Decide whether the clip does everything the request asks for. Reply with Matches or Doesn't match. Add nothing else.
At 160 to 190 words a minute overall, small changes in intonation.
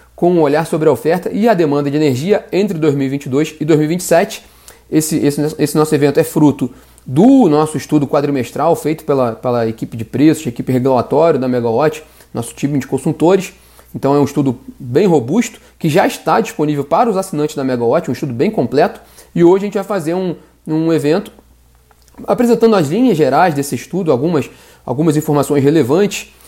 Doesn't match